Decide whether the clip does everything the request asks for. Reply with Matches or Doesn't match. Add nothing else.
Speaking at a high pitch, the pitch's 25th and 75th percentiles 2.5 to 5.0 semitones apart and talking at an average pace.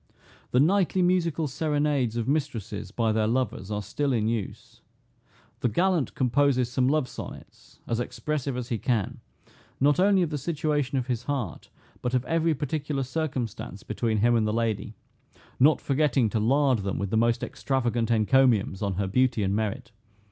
Doesn't match